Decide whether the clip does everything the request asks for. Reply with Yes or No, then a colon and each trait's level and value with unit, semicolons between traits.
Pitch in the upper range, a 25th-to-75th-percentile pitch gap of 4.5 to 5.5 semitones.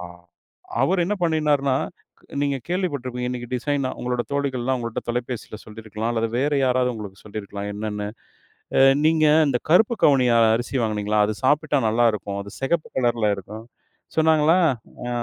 No: low, 125 Hz; average, 4.9 semitones